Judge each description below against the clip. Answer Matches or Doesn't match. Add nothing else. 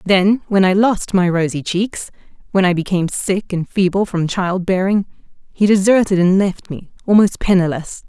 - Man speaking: Doesn't match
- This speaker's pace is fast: Doesn't match